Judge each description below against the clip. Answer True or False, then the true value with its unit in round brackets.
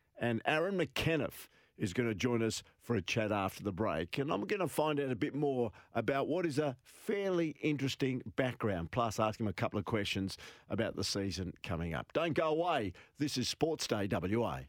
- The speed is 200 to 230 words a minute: True (205 wpm)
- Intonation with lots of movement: True (5.9 semitones)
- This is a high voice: False (120 Hz)